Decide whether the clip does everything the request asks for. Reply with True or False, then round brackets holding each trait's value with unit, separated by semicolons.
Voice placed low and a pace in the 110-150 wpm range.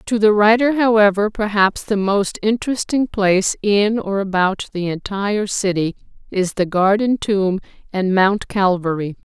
False (200 Hz; 140 wpm)